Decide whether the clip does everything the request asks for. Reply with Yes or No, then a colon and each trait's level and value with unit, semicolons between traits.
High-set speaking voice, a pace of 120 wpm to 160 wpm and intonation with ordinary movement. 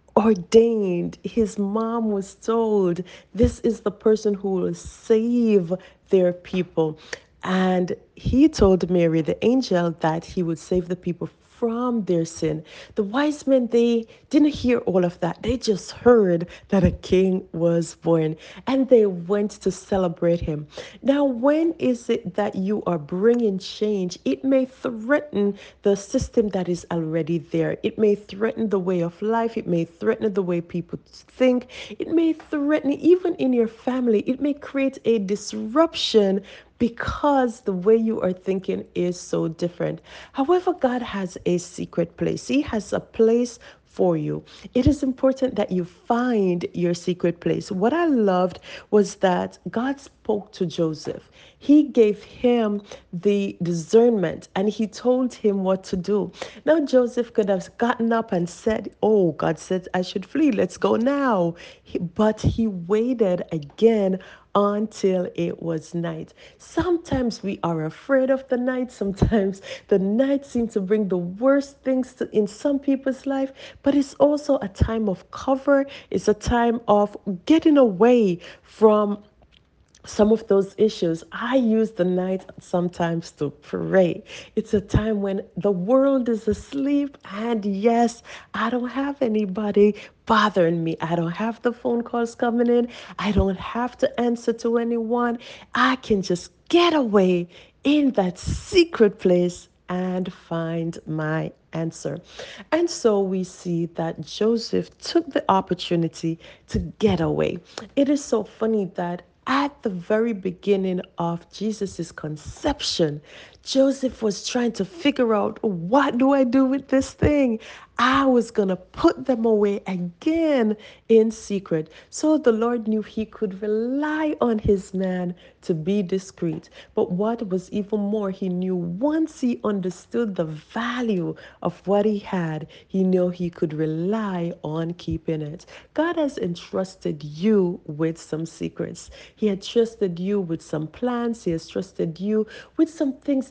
Yes: high, 210 Hz; average, 155 wpm; average, 5.0 semitones